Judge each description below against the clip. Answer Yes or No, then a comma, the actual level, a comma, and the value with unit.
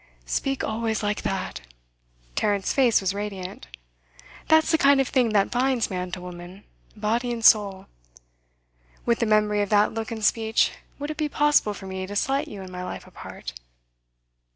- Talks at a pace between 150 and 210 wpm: Yes, average, 175 wpm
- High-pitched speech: Yes, high, 210 Hz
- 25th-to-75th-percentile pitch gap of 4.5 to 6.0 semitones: No, average, 3.9 semitones